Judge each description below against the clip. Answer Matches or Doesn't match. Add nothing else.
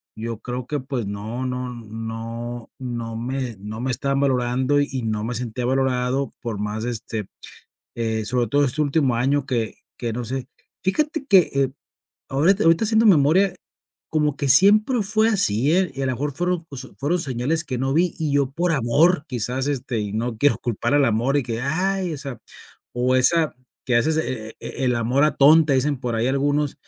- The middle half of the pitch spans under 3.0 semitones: Doesn't match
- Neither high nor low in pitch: Doesn't match